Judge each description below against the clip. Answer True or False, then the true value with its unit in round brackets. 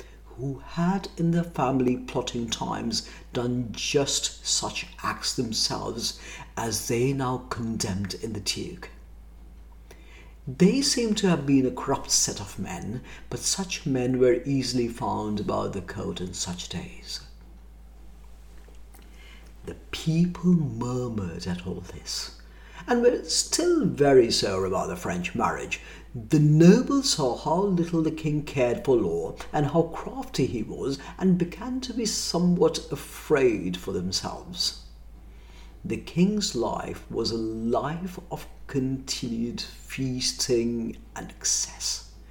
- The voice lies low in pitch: True (125 Hz)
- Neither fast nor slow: False (130 wpm)